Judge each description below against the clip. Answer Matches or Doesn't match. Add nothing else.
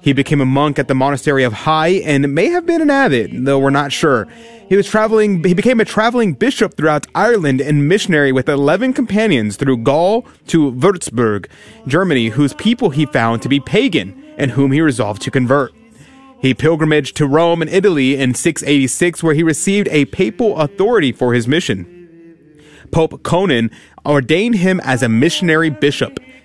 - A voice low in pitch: Doesn't match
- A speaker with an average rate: Matches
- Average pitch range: Doesn't match